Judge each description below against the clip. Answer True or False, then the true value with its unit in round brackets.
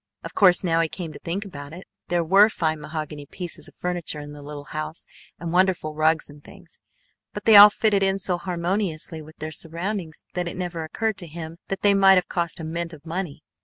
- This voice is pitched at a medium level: True (170 Hz)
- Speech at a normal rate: False (220 wpm)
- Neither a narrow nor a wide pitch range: True (3.3 semitones)